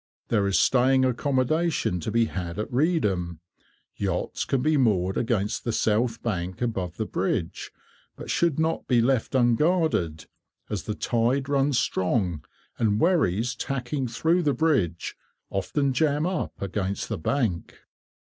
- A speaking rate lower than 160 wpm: Yes, average, 140 wpm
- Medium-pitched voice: No, low, 120 Hz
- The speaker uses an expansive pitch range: Yes, wide, 6.3 semitones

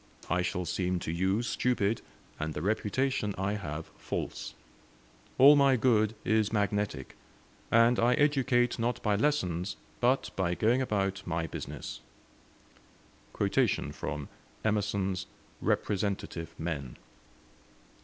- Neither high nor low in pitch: No, low, 105 Hz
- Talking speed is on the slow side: Yes, slow, 105 wpm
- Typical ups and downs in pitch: Yes, average, 5.0 semitones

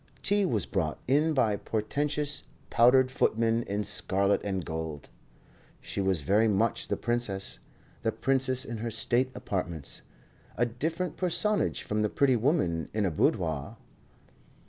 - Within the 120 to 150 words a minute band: Yes, average, 140 wpm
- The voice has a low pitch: Yes, low, 115 Hz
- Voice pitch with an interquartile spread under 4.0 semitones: No, wide, 5.4 semitones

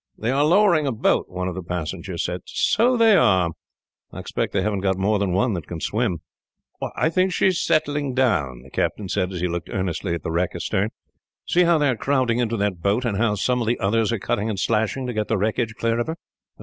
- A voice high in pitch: No, low, 110 Hz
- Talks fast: Yes, fast, 240 wpm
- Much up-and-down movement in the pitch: Yes, wide, 5.8 semitones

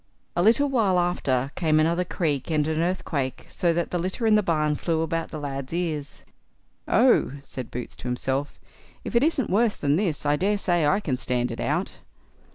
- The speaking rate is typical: Yes, average, 190 wpm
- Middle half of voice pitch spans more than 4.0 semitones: Yes, average, 4.4 semitones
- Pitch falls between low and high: Yes, medium, 165 Hz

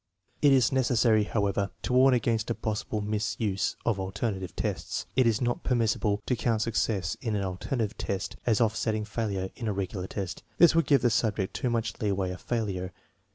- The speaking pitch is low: Yes, low, 110 Hz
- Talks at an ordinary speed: Yes, average, 185 wpm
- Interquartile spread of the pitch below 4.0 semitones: Yes, average, 3.1 semitones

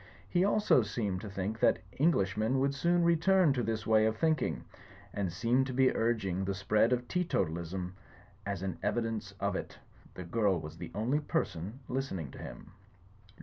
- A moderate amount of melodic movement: No, wide, 5.9 semitones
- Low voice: Yes, low, 110 Hz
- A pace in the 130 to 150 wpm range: No, average, 175 wpm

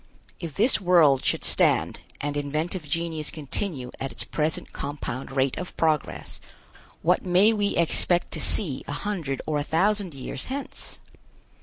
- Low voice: No, medium, 160 Hz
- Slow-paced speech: No, average, 150 wpm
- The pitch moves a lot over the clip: No, average, 4.3 semitones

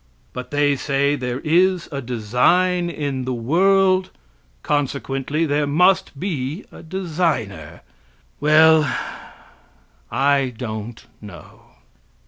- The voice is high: No, medium, 145 Hz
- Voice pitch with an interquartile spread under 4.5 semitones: No, average, 4.9 semitones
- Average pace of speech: No, slow, 100 wpm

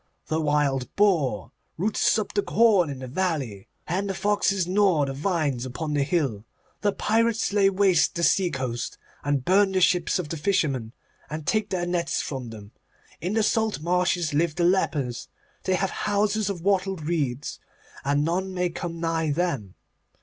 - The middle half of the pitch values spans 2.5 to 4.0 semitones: No, average, 5.1 semitones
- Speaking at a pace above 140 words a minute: Yes, average, 170 wpm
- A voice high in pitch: No, medium, 170 Hz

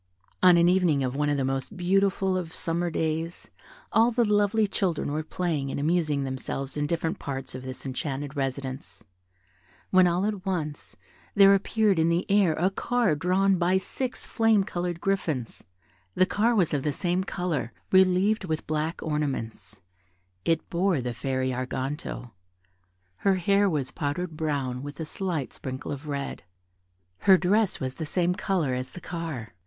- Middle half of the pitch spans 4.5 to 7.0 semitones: Yes, average, 5.1 semitones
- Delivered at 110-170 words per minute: Yes, average, 165 wpm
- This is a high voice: No, medium, 165 Hz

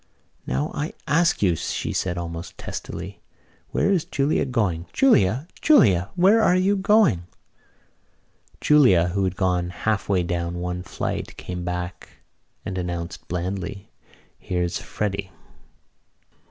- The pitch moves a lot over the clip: Yes, wide, 7.7 semitones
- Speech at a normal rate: No, slow, 125 wpm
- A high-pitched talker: No, very low, 95 Hz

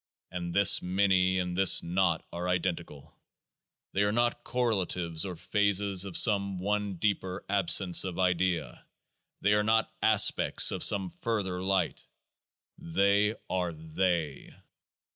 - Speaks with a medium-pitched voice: No, very low, 95 Hz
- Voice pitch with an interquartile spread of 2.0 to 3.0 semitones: Yes, narrow, 2.4 semitones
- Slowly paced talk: Yes, slow, 125 wpm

